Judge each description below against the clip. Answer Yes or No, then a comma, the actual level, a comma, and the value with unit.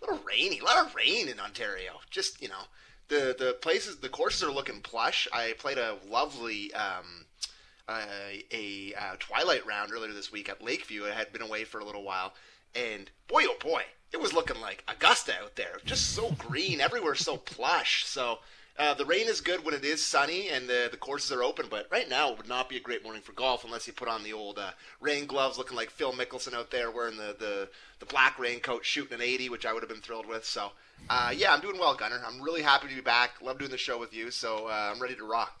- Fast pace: Yes, fast, 245 wpm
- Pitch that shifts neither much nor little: No, wide, 6.7 semitones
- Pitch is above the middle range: No, low, 125 Hz